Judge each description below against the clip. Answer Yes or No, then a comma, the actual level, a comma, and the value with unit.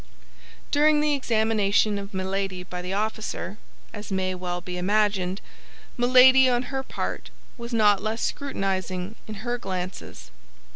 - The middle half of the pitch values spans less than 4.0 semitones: No, average, 4.3 semitones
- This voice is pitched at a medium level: No, high, 205 Hz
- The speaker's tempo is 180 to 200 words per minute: No, slow, 135 wpm